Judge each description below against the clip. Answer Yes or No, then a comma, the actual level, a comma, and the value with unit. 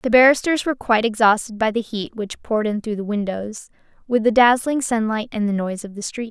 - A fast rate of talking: Yes, fast, 230 wpm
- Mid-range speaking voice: No, high, 220 Hz